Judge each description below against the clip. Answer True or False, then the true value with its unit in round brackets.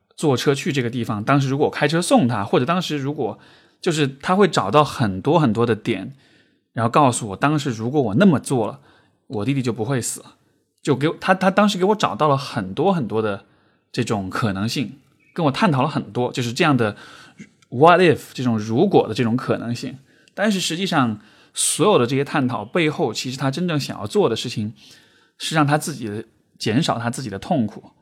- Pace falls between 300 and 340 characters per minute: True (310 characters per minute)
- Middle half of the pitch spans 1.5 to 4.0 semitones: False (4.6 semitones)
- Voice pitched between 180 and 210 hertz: False (135 Hz)